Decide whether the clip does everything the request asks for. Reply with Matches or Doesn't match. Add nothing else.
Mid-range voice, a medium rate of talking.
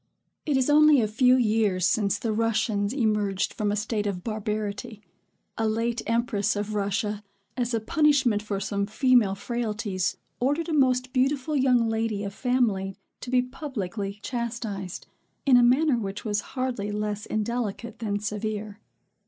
Doesn't match